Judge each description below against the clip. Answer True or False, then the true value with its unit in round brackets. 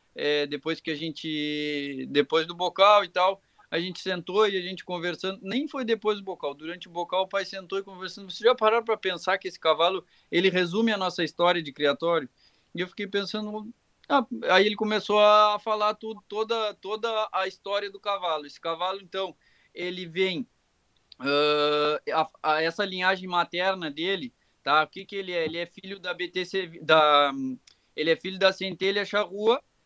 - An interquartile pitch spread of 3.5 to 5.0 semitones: True (3.9 semitones)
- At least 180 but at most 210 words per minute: True (185 wpm)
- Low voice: False (185 Hz)